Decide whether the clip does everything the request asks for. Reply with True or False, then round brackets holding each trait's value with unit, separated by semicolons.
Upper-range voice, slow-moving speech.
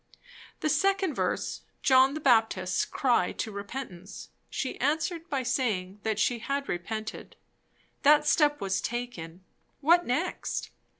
True (255 Hz; 125 wpm)